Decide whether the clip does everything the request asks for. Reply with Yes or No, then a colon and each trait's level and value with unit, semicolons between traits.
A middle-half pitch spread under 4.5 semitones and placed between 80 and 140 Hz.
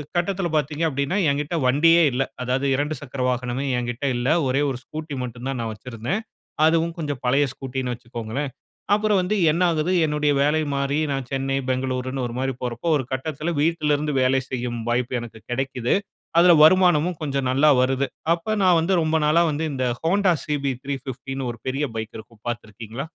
Yes: average, 3.7 semitones; low, 135 Hz